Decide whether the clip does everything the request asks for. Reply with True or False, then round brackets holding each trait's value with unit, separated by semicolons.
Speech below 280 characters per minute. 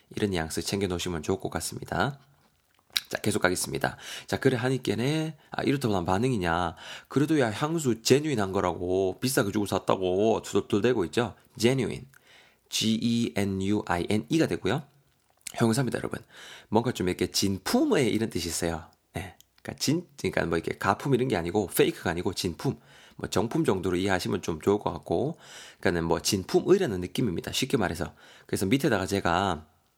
False (390 characters per minute)